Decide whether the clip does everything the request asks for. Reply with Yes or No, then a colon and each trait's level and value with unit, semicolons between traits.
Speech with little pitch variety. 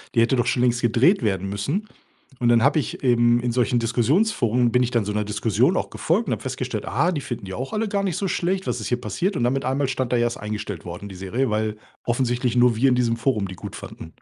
No: average, 3.5 semitones